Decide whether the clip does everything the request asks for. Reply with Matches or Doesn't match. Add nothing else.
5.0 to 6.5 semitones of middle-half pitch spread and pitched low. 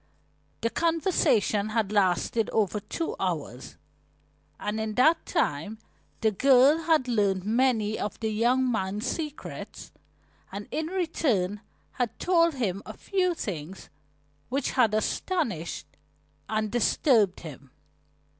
Doesn't match